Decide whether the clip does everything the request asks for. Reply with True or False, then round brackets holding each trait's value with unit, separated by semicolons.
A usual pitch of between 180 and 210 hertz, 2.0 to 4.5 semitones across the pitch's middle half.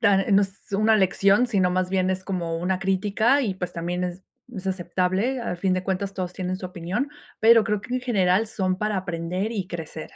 True (190 Hz; 2.6 semitones)